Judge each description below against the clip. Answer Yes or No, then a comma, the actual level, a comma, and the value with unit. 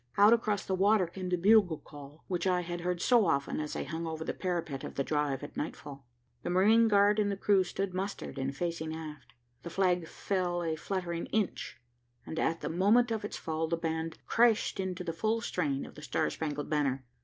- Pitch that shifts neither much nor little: Yes, average, 3.9 semitones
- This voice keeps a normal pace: No, fast, 210 wpm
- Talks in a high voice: No, medium, 175 Hz